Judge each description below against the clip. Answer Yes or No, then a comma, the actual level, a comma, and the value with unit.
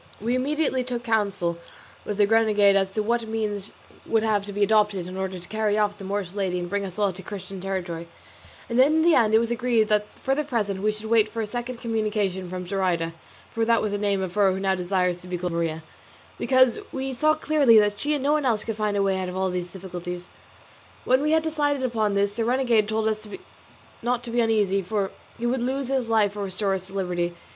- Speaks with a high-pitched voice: Yes, high, 210 Hz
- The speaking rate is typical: No, fast, 235 wpm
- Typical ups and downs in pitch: Yes, average, 3.6 semitones